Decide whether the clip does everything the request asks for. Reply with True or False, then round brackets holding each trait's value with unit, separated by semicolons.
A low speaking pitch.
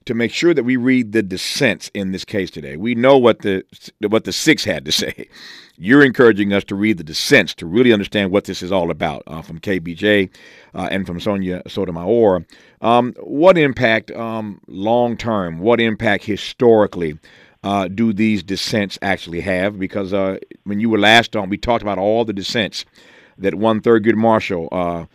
True (105 Hz)